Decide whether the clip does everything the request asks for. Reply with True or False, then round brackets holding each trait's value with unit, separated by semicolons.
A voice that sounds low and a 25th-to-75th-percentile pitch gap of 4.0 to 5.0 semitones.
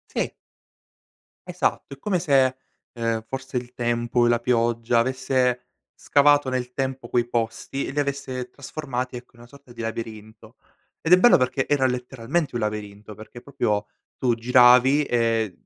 False (125 Hz; 2.4 semitones)